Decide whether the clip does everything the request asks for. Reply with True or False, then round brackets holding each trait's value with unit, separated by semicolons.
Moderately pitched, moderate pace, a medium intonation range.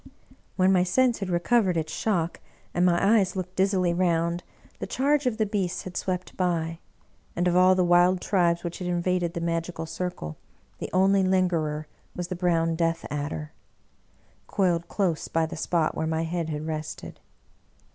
False (175 Hz; 175 wpm; 2.0 semitones)